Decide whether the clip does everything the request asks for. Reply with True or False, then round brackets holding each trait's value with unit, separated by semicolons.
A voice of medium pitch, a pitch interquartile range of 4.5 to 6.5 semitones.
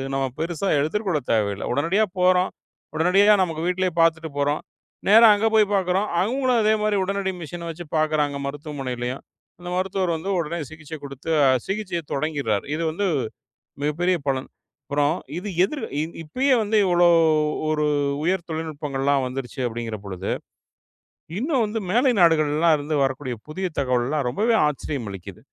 True (160 Hz; 5.1 semitones)